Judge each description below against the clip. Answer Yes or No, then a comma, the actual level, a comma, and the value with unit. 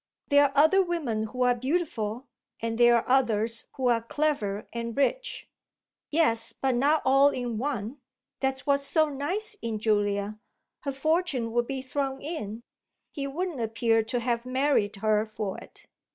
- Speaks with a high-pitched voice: Yes, very high, 255 Hz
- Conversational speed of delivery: Yes, average, 160 wpm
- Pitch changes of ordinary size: Yes, average, 4.1 semitones